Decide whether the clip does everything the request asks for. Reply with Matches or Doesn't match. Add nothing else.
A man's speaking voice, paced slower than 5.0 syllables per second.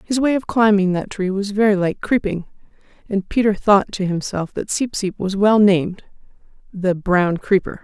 Doesn't match